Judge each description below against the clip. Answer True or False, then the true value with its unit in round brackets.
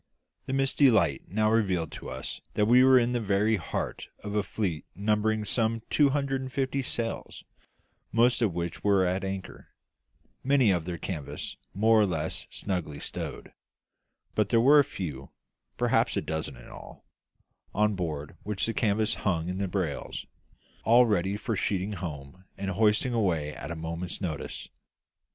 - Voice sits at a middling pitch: False (100 Hz)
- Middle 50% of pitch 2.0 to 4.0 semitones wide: False (4.7 semitones)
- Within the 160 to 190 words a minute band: True (165 wpm)